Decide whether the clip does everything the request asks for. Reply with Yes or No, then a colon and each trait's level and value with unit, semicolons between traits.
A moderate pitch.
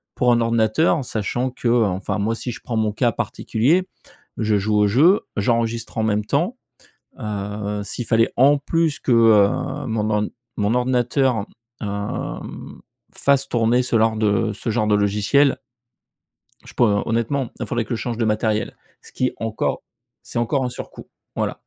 No: low, 115 Hz